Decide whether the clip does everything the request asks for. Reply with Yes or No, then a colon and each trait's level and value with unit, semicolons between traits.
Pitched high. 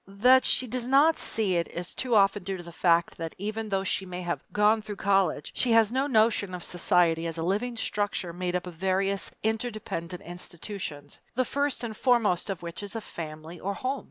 Yes: high, 195 Hz